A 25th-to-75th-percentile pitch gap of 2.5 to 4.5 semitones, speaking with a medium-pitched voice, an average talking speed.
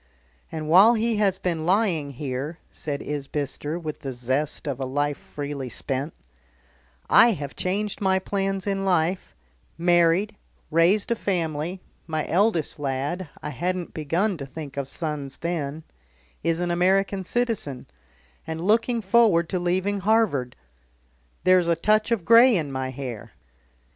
No: average, 5.0 semitones; medium, 170 Hz; average, 145 wpm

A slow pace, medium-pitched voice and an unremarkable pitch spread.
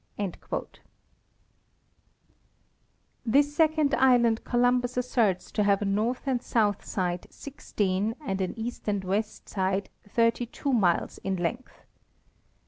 No: slow, 120 wpm; high, 225 Hz; average, 4.2 semitones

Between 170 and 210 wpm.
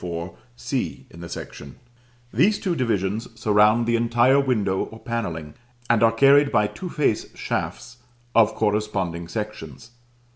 No: average, 140 wpm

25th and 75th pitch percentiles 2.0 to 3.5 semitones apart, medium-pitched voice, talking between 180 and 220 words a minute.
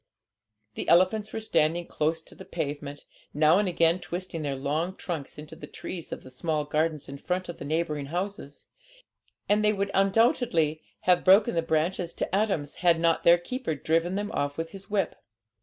No: average, 3.9 semitones; medium, 170 Hz; average, 185 wpm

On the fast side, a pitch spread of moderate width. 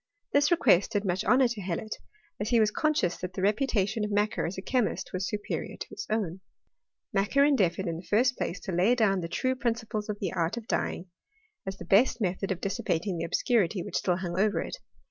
Yes: fast, 220 wpm; average, 3.9 semitones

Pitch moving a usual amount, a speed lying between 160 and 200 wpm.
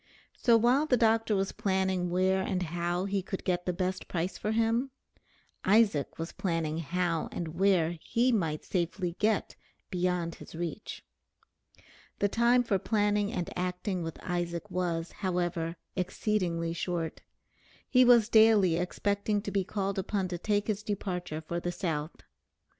No: average, 3.2 semitones; average, 150 wpm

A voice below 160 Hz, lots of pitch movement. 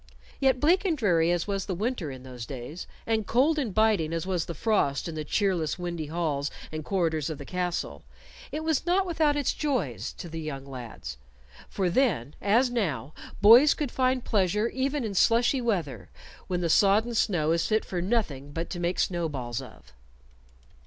No: medium, 180 Hz; wide, 7.2 semitones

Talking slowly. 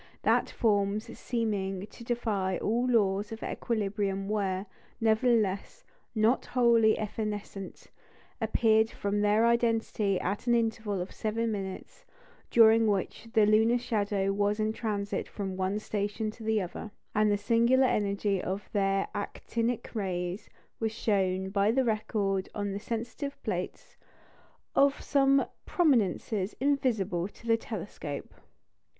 Yes: slow, 130 wpm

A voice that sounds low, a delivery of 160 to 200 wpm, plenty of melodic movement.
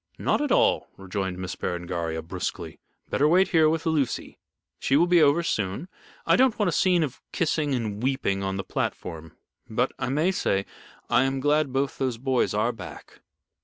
Yes: low, 130 Hz; average, 180 wpm; wide, 8.2 semitones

